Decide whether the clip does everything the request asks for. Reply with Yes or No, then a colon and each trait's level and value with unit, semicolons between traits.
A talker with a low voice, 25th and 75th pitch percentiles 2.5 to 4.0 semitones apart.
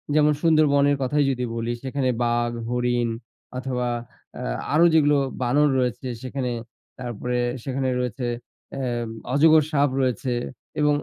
Yes: low, 130 Hz; average, 2.9 semitones